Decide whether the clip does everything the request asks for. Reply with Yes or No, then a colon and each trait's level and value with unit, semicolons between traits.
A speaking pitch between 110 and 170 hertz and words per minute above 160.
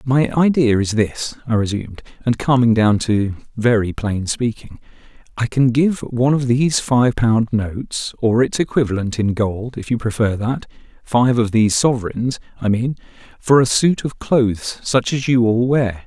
Yes: low, 120 Hz; average, 170 wpm